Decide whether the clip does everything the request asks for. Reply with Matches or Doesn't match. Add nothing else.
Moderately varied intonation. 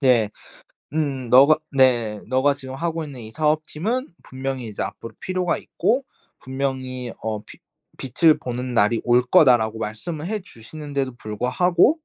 Matches